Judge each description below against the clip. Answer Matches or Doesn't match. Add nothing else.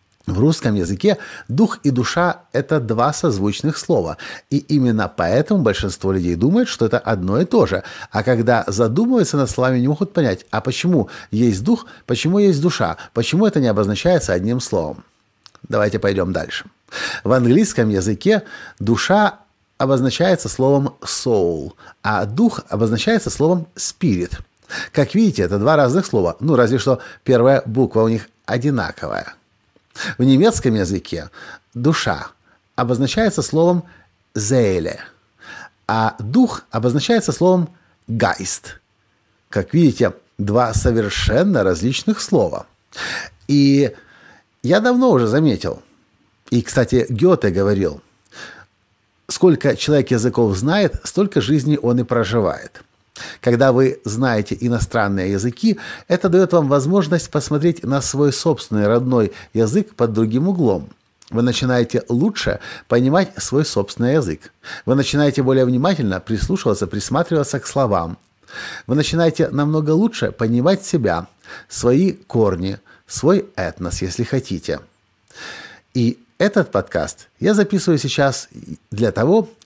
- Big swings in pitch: Matches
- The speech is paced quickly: Doesn't match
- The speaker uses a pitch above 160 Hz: Doesn't match